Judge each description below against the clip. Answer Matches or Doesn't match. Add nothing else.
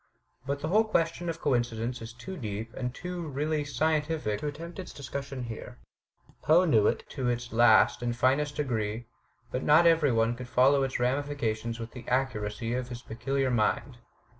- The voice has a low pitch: Matches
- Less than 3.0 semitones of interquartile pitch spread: Doesn't match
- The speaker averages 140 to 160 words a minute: Doesn't match